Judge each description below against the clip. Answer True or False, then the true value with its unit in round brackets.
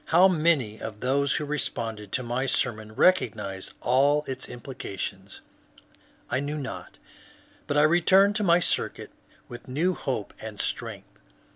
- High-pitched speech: False (130 Hz)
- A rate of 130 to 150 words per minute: True (140 wpm)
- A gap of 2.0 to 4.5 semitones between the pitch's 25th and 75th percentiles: False (5.6 semitones)